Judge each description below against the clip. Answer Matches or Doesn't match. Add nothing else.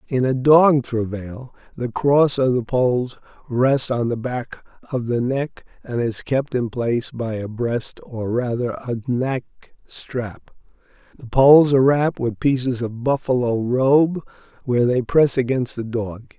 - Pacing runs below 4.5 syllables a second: Matches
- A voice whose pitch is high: Doesn't match